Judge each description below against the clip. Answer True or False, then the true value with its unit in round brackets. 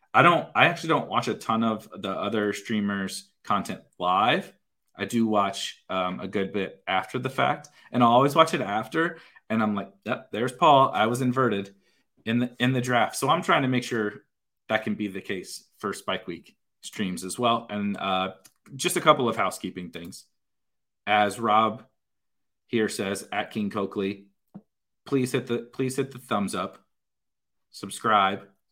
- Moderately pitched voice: False (110 Hz)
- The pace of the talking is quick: False (180 wpm)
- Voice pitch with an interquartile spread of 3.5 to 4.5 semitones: True (3.9 semitones)